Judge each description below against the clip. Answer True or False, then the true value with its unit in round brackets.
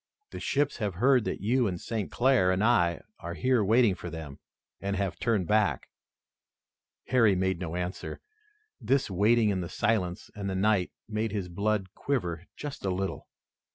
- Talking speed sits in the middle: True (170 wpm)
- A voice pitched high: False (100 Hz)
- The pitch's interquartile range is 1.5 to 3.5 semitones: False (3.9 semitones)